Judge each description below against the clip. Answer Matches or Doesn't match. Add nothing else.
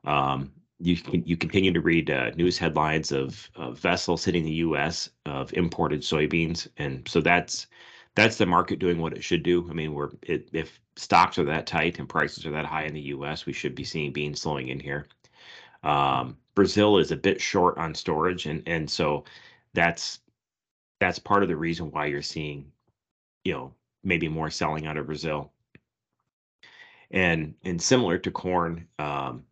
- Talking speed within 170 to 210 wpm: Matches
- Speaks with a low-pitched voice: Matches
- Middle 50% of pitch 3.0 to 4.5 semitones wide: Doesn't match